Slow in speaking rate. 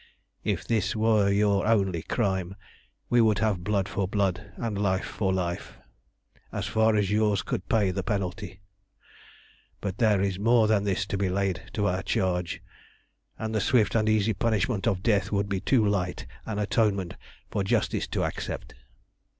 No: average, 165 wpm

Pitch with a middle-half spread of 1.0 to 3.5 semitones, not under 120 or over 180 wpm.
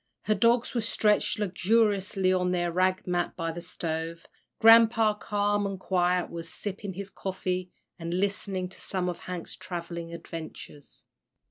Yes: average, 2.8 semitones; average, 145 wpm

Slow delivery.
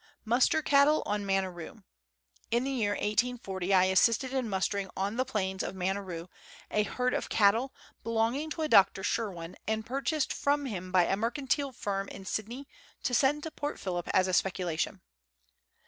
No: average, 165 wpm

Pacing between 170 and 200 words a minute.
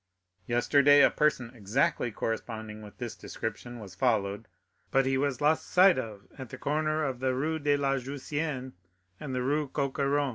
Yes: average, 175 wpm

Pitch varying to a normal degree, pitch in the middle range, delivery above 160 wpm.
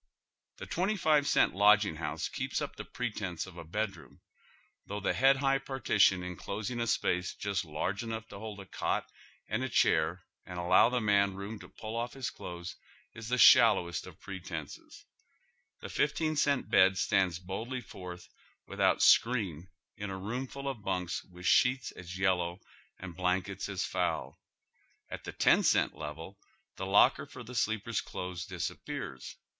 No: average, 4.6 semitones; low, 100 Hz; average, 170 wpm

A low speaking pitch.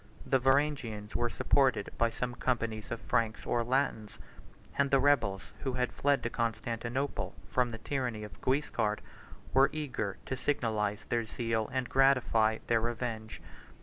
Yes: low, 120 Hz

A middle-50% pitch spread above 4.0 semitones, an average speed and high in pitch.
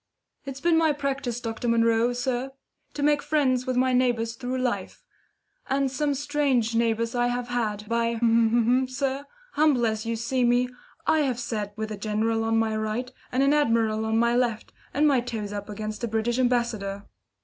No: average, 2.7 semitones; average, 180 wpm; high, 240 Hz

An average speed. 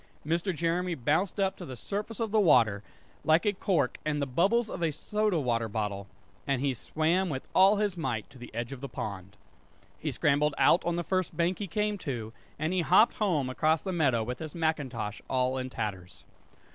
No: fast, 210 wpm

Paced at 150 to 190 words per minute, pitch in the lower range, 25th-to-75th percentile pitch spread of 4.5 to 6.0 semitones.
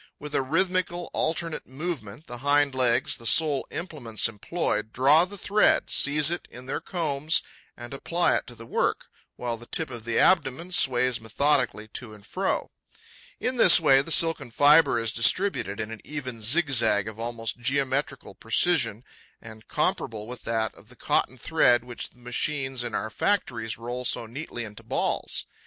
Yes: average, 170 wpm; low, 130 Hz; average, 5.2 semitones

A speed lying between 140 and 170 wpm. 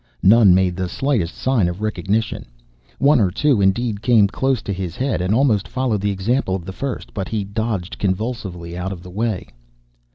No: average, 190 wpm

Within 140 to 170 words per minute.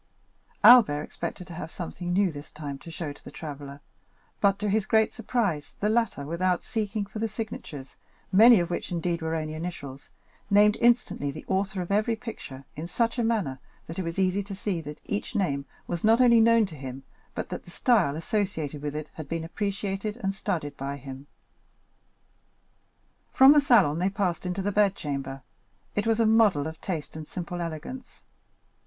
No: average, 185 wpm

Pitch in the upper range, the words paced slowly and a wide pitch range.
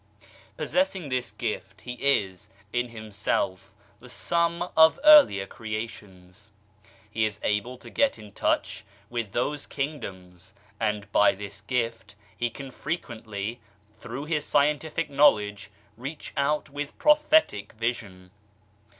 No: low, 115 Hz; slow, 120 wpm; wide, 6.0 semitones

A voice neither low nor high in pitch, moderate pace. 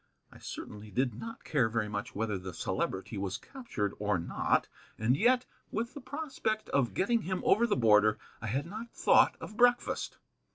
No: low, 125 Hz; average, 175 wpm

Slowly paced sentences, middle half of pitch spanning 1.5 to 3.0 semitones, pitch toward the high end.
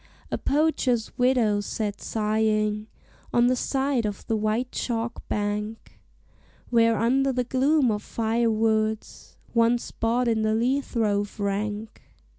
Yes: slow, 130 wpm; narrow, 2.5 semitones; high, 225 Hz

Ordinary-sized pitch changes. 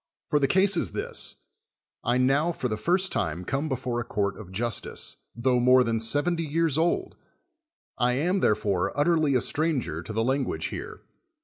No: wide, 5.7 semitones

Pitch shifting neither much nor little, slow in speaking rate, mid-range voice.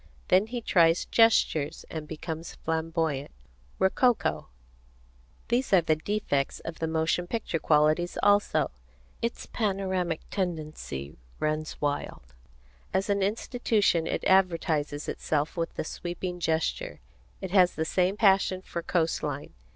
Yes: average, 3.6 semitones; slow, 125 wpm; medium, 170 Hz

